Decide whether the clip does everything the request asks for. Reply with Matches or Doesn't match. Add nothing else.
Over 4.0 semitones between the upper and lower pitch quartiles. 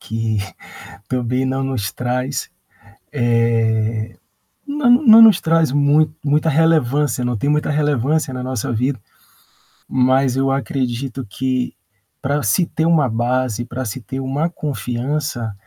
Doesn't match